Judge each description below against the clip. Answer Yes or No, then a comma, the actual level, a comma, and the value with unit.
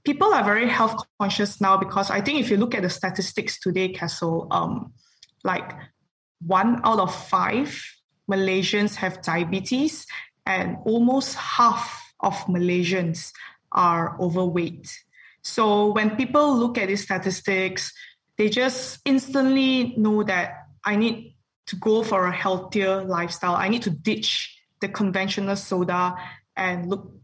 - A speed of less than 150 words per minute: Yes, slow, 135 wpm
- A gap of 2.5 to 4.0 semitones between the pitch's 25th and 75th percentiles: Yes, average, 3.6 semitones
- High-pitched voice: Yes, high, 195 Hz